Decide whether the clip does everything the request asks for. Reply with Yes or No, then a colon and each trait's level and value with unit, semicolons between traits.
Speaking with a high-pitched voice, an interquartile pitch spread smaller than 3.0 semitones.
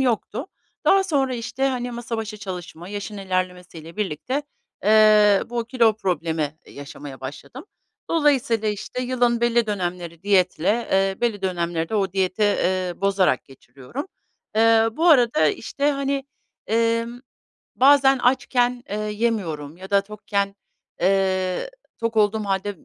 No: high, 210 Hz; average, 4.5 semitones